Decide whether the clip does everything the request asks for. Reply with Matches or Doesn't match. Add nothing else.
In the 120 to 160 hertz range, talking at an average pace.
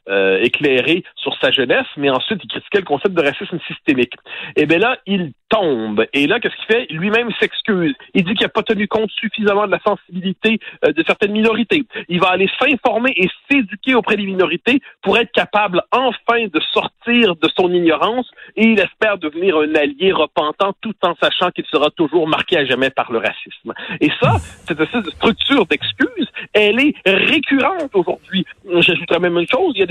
Doesn't match